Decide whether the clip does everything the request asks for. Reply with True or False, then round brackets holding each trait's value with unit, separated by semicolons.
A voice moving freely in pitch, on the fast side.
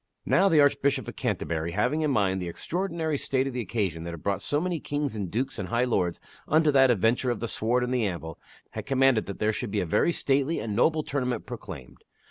True (6.0 semitones; 230 wpm)